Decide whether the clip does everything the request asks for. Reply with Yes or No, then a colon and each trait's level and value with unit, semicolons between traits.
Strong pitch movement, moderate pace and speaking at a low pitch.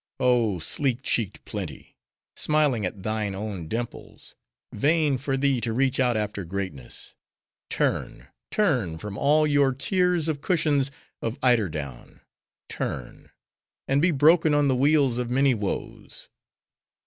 No: wide, 5.7 semitones; slow, 125 wpm; low, 125 Hz